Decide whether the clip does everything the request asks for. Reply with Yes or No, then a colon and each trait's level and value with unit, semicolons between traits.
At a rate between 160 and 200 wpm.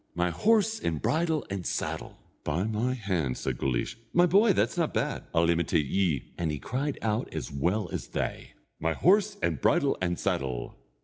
Yes: average, 180 wpm